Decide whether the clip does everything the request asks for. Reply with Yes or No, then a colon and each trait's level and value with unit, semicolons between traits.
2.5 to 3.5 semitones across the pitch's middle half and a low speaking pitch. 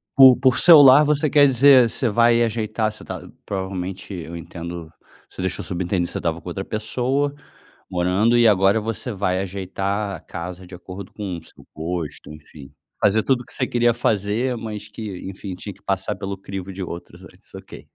No: average, 4.4 semitones; low, 100 Hz